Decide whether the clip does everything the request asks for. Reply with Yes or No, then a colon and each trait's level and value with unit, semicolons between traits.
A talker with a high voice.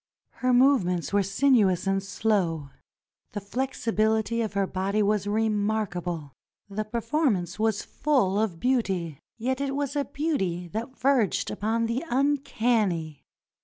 Yes: high, 215 Hz